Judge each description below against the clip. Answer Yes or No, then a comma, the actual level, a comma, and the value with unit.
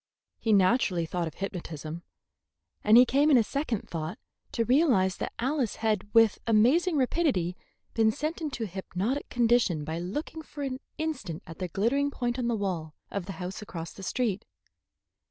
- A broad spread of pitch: Yes, wide, 6.3 semitones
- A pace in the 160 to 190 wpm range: Yes, average, 175 wpm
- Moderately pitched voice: No, high, 220 Hz